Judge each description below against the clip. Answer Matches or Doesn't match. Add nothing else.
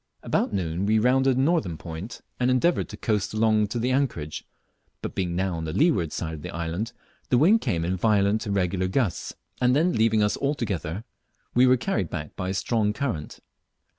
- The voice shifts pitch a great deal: Matches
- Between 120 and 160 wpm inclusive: Doesn't match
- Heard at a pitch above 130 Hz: Doesn't match